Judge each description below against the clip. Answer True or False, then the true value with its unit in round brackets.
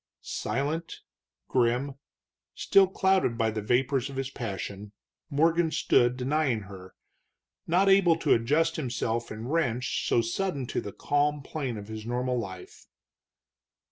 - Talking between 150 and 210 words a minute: False (135 wpm)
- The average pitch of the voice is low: True (130 Hz)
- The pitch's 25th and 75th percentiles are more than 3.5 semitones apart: True (5.4 semitones)